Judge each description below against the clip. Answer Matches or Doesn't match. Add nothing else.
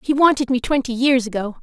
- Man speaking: Doesn't match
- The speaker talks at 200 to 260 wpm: Matches